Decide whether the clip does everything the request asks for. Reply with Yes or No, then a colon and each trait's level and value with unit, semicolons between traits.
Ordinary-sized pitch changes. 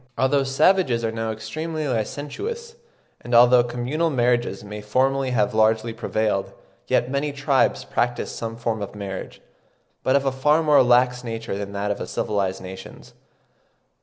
Yes: average, 4.0 semitones